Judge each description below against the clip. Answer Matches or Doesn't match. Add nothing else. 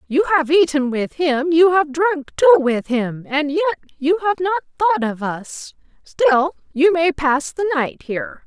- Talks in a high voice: Matches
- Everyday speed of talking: Matches